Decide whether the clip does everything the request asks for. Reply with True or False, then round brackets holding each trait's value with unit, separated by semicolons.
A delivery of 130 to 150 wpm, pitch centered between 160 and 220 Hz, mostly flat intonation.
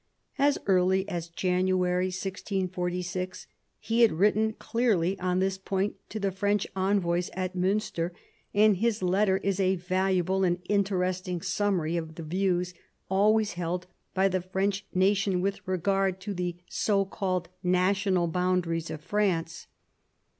True (140 wpm; 185 Hz; 1.6 semitones)